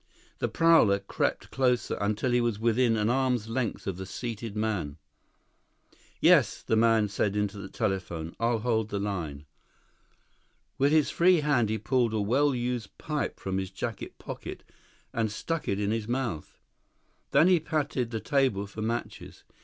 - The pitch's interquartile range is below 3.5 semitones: No, average, 3.8 semitones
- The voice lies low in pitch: Yes, low, 110 Hz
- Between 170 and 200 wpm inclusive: No, average, 160 wpm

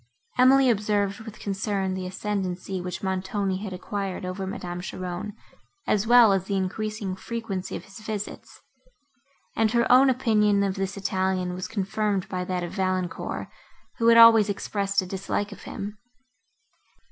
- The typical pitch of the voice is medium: No, high, 195 Hz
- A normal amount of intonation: No, narrow, 2.3 semitones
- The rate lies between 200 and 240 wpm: No, average, 150 wpm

